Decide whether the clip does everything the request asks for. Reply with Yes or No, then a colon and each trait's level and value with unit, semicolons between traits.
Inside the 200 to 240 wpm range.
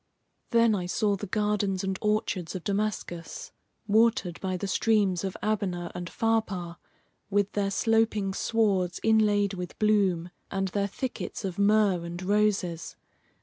No: average, 140 wpm